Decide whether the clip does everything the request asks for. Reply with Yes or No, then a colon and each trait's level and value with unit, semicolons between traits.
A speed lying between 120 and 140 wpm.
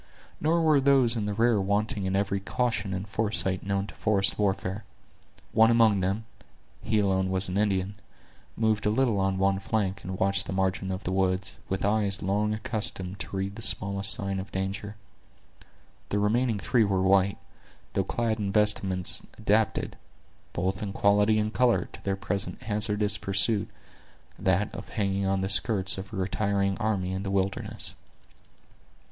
No: average, 165 wpm